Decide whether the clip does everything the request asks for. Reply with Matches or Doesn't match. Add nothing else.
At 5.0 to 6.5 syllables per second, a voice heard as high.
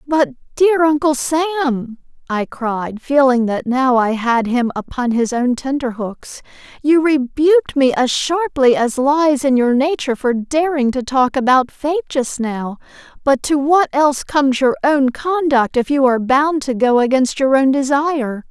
Doesn't match